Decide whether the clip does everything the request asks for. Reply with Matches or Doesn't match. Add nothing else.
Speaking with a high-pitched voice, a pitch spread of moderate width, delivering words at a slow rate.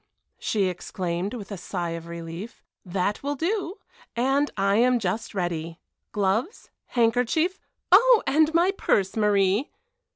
Doesn't match